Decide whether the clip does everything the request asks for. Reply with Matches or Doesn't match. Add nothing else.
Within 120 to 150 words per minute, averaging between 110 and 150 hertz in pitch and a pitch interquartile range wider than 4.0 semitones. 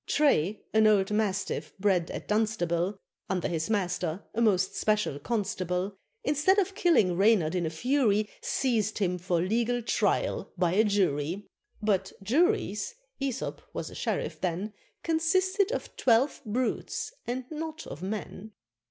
Doesn't match